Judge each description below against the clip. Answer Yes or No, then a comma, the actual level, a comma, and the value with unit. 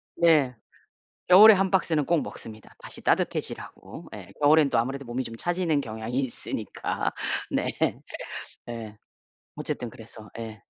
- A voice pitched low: Yes, low, 130 Hz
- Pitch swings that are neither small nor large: No, wide, 6.2 semitones